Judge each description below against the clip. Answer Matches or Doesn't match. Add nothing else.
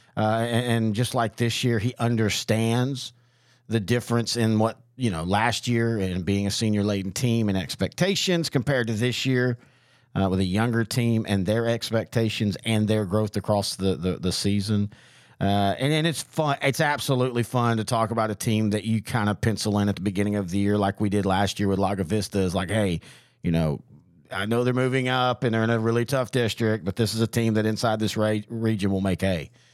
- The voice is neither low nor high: Doesn't match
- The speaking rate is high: Matches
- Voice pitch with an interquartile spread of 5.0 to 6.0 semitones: Doesn't match